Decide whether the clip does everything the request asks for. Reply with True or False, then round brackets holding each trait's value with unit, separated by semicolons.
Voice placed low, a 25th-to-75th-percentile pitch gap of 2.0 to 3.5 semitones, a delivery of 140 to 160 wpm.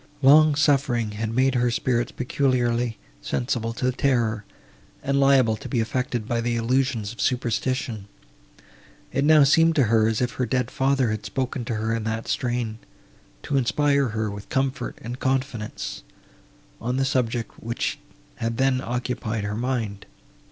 True (120 Hz; 2.8 semitones; 150 wpm)